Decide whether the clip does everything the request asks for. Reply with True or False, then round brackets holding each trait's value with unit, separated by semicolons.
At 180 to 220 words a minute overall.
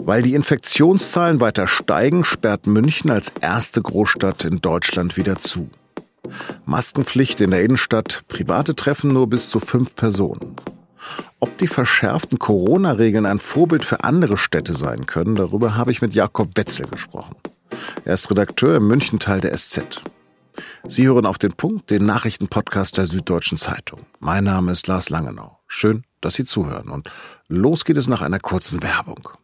False (155 wpm)